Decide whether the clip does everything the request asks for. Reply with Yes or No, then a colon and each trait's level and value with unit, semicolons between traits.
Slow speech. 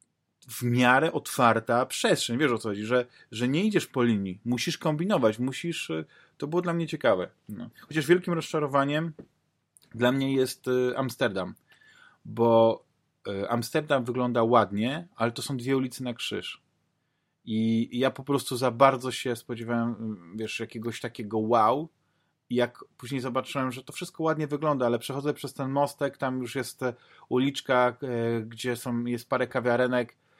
No: average, 150 wpm